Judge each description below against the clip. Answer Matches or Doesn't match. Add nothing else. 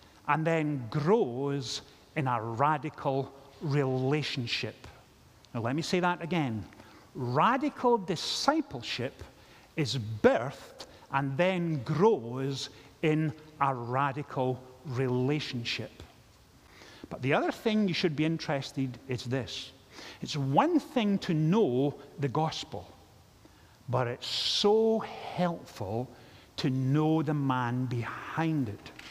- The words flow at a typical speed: Doesn't match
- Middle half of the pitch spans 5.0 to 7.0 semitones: Doesn't match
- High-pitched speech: Doesn't match